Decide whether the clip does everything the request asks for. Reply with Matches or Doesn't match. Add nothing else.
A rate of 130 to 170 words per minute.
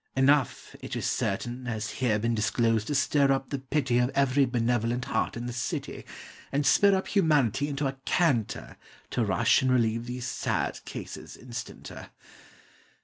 Matches